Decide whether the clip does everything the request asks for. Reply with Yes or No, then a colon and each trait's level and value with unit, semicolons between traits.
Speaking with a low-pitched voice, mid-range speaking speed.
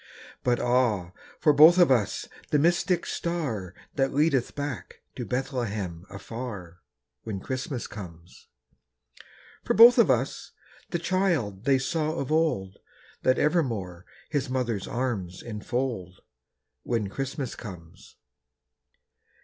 No: low, 125 Hz; slow, 115 wpm